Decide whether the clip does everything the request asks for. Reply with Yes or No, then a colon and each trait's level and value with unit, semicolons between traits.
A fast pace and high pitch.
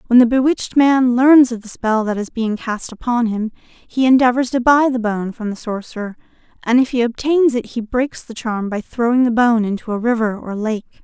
Yes: fast, 225 wpm; high, 235 Hz